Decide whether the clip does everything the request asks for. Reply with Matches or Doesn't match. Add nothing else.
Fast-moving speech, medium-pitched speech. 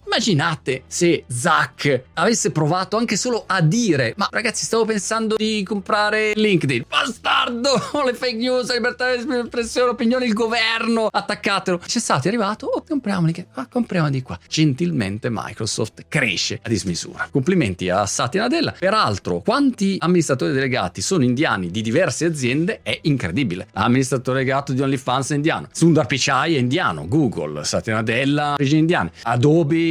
Doesn't match